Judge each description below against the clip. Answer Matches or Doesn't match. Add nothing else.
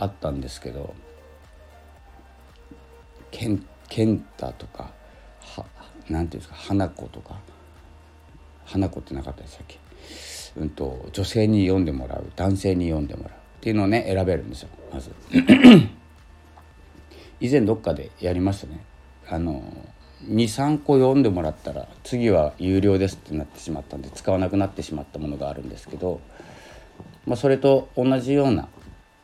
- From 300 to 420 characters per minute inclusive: Matches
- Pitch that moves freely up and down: Doesn't match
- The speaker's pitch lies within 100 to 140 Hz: Doesn't match